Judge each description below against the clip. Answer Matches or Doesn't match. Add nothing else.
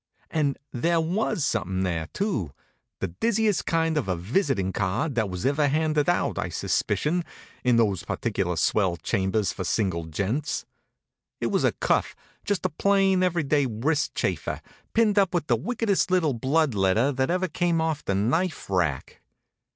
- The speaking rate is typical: Matches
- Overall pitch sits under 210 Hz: Matches